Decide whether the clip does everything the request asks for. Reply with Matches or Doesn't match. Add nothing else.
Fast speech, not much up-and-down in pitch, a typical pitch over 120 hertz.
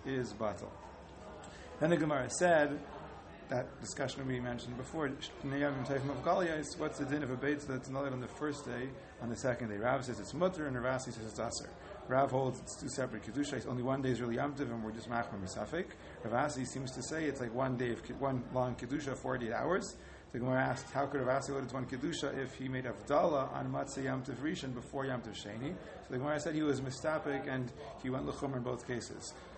Matches